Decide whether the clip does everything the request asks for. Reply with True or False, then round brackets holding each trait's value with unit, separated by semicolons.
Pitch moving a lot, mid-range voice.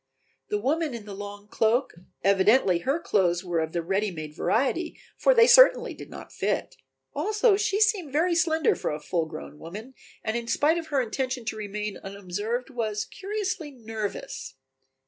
False (8.4 semitones; 230 Hz)